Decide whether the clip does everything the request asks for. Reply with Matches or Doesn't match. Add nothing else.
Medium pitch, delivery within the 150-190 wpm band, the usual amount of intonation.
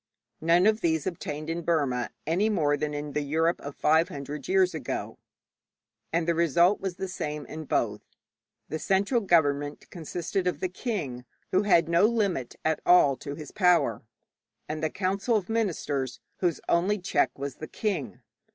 Matches